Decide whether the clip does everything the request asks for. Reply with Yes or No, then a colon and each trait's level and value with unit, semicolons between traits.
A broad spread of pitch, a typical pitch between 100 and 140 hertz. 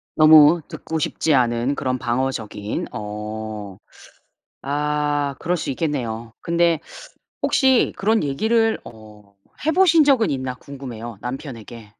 Yes: wide, 6.0 semitones; low, 135 Hz